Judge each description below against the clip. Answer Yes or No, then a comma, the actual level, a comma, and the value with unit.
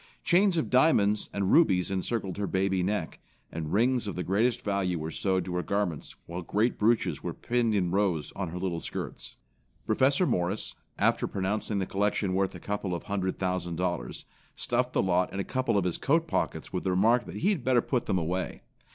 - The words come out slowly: No, fast, 205 wpm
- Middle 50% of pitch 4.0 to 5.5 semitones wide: Yes, average, 4.3 semitones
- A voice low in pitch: Yes, low, 100 Hz